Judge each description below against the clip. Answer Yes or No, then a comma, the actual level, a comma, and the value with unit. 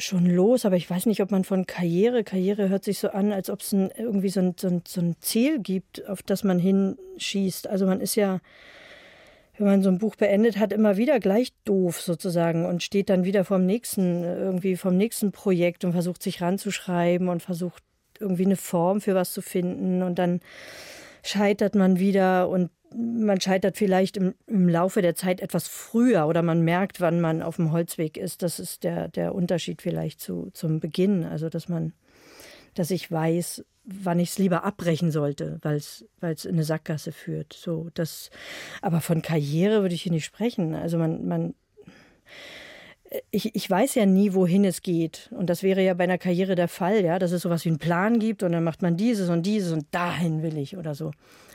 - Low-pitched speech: No, medium, 185 Hz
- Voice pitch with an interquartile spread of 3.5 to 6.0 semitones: No, average, 2.8 semitones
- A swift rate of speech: Yes, fast, 205 wpm